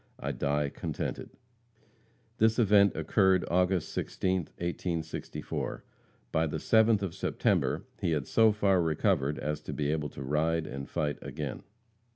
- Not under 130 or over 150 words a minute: Yes, average, 140 wpm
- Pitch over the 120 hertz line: No, very low, 85 Hz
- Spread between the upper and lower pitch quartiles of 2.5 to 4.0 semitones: No, average, 4.5 semitones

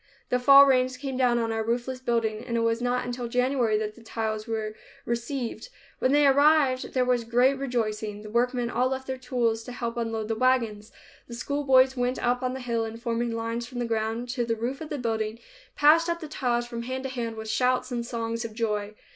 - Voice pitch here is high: Yes, high, 240 Hz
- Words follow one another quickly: Yes, fast, 220 wpm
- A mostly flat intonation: Yes, narrow, 2.1 semitones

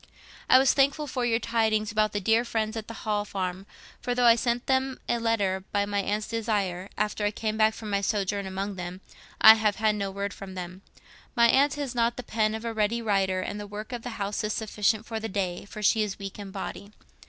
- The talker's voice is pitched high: Yes, high, 215 Hz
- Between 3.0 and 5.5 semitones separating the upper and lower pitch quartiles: No, narrow, 2.4 semitones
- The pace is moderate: No, fast, 235 wpm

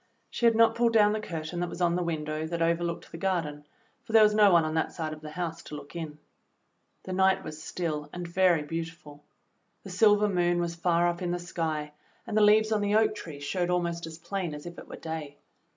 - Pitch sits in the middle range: Yes, medium, 170 Hz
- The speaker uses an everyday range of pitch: Yes, average, 3.2 semitones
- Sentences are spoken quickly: Yes, fast, 240 wpm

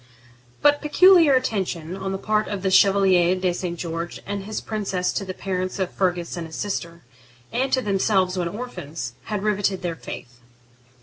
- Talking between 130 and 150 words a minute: No, average, 175 wpm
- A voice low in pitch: No, high, 190 Hz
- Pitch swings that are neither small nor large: Yes, average, 3.0 semitones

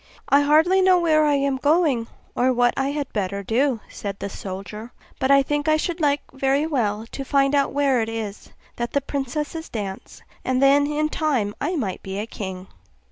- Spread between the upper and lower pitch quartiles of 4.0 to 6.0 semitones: Yes, average, 4.7 semitones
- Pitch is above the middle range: Yes, very high, 275 Hz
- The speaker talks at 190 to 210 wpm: Yes, average, 195 wpm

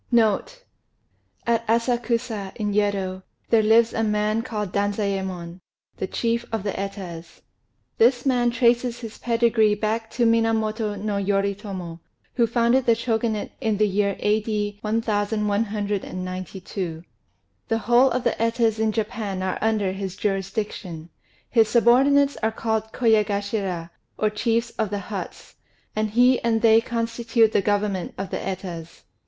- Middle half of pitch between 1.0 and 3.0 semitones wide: Yes, narrow, 2.5 semitones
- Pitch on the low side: No, high, 215 Hz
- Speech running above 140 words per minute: No, slow, 135 wpm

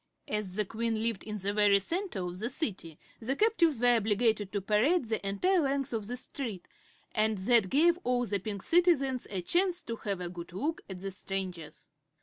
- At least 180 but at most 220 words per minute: Yes, average, 195 wpm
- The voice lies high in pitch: Yes, high, 220 Hz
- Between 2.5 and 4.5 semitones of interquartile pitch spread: No, wide, 5.5 semitones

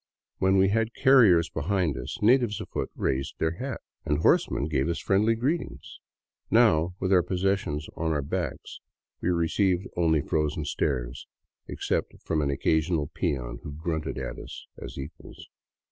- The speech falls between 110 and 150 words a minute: No, average, 160 wpm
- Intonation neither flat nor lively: Yes, average, 4.5 semitones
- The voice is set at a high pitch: No, very low, 85 Hz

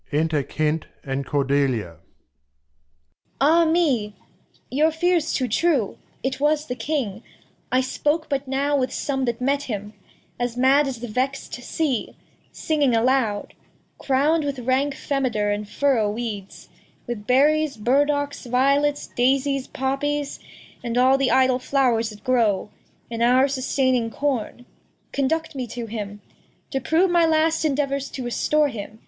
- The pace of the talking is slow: Yes, slow, 125 wpm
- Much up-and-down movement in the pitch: No, average, 3.9 semitones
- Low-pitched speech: No, very high, 260 Hz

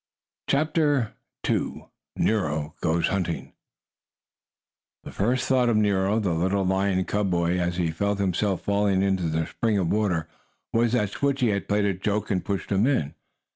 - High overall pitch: No, low, 100 Hz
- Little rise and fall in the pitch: No, average, 3.0 semitones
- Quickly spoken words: No, average, 160 wpm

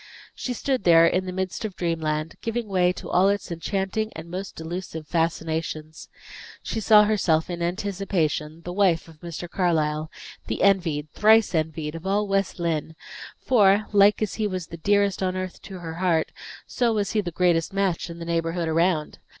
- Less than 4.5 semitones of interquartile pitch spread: Yes, average, 3.4 semitones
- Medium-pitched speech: Yes, medium, 180 Hz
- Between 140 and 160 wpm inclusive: No, average, 180 wpm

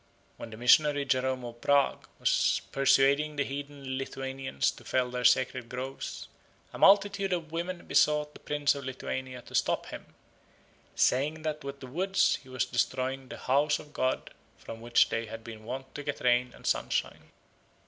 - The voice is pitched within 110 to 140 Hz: Yes, low, 135 Hz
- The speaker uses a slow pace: No, average, 170 wpm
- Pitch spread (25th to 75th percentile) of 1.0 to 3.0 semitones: Yes, average, 2.7 semitones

